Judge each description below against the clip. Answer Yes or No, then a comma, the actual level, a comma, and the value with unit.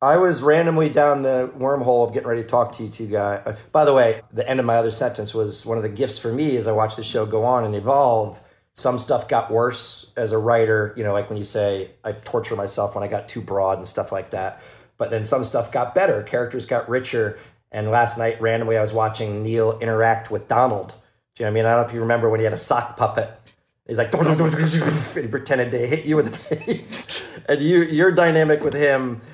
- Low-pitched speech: Yes, low, 115 Hz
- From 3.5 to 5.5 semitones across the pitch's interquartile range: Yes, average, 3.8 semitones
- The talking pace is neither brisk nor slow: No, fast, 250 wpm